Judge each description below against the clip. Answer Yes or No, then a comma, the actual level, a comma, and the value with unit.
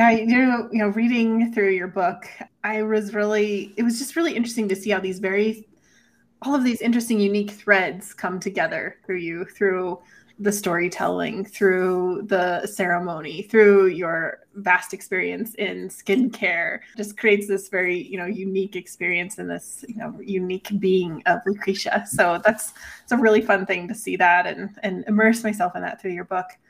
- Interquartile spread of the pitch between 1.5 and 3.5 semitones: Yes, average, 3.0 semitones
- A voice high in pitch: Yes, high, 200 Hz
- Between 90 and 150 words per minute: No, average, 175 wpm